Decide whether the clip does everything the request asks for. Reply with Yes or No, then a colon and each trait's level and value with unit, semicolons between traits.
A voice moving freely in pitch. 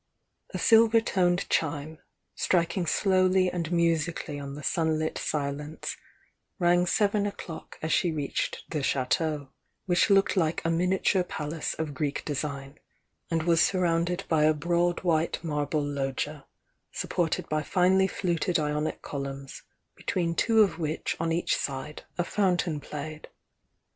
No: average, 3.0 semitones